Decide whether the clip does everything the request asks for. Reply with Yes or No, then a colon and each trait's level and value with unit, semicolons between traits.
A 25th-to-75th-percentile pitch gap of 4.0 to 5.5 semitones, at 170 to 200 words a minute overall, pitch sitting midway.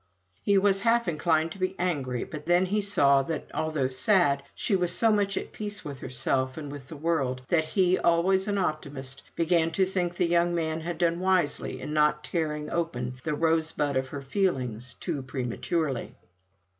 Yes: average, 4.6 semitones; average, 180 wpm; medium, 160 Hz